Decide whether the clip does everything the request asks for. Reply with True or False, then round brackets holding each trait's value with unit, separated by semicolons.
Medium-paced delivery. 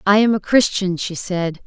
False (215 wpm)